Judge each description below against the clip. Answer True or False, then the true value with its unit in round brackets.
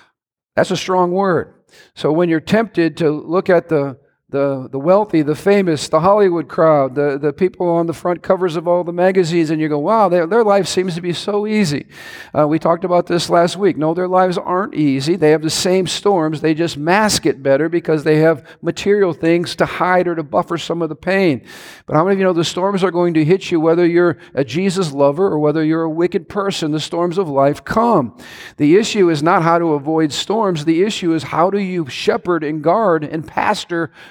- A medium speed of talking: False (225 wpm)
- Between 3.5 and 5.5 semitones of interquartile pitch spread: False (2.8 semitones)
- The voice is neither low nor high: True (170 Hz)